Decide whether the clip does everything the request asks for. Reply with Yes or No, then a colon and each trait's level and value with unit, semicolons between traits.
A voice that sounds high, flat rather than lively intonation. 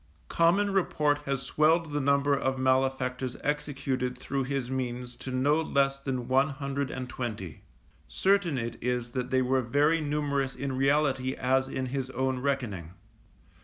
No: low, 135 Hz; narrow, 2.0 semitones